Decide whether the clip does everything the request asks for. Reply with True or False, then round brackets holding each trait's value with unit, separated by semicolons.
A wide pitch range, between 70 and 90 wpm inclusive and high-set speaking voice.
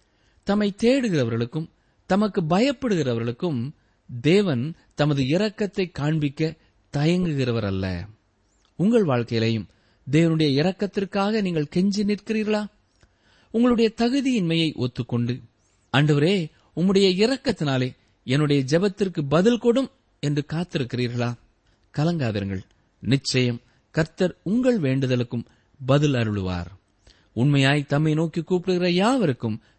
False (8.2 semitones; 80 wpm; 145 Hz)